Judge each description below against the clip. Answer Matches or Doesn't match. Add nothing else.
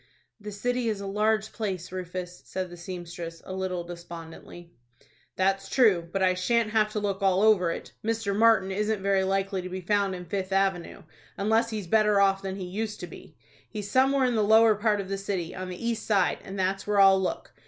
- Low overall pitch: Doesn't match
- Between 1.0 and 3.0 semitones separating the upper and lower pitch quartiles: Matches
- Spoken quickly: Matches